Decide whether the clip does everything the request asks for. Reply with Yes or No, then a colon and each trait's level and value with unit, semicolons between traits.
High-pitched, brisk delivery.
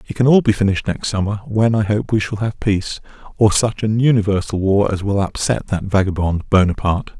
No: low, 105 Hz; fast, 210 wpm